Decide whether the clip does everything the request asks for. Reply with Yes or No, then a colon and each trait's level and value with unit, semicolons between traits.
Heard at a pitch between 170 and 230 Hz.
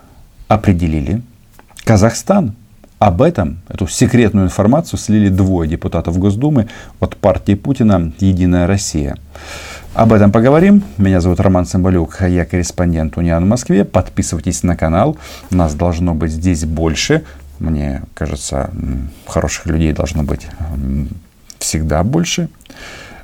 No: very low, 90 Hz